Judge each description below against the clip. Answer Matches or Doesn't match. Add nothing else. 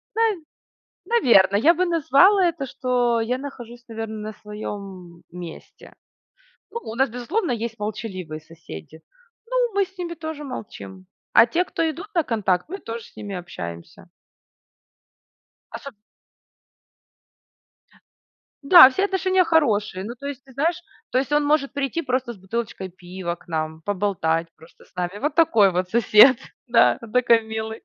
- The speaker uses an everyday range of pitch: Doesn't match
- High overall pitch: Matches